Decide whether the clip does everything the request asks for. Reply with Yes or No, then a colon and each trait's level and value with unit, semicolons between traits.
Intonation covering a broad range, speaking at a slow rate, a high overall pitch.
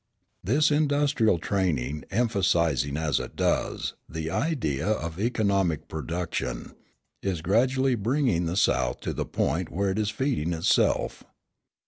No: wide, 6.8 semitones; slow, 125 wpm; very low, 95 Hz